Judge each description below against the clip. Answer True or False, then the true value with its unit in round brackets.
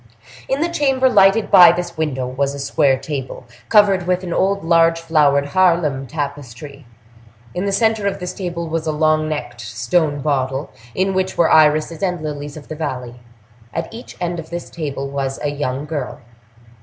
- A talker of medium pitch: True (155 Hz)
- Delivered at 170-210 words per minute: True (180 wpm)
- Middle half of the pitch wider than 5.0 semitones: False (4.1 semitones)